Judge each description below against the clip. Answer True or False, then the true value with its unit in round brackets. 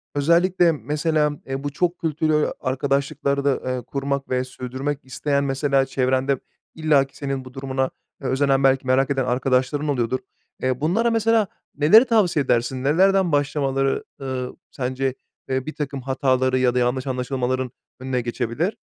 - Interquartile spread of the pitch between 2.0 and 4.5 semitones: True (2.4 semitones)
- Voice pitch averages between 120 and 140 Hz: True (135 Hz)